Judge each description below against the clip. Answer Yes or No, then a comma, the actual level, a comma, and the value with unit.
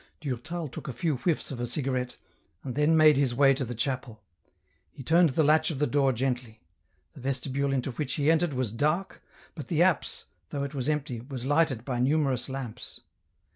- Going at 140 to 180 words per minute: No, average, 195 wpm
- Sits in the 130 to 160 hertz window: Yes, low, 135 Hz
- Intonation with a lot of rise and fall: No, average, 3.3 semitones